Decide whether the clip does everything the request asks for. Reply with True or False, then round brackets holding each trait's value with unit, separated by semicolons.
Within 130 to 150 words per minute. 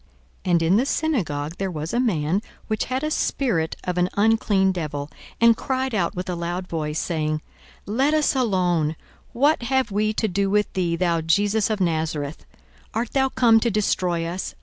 False (190 wpm)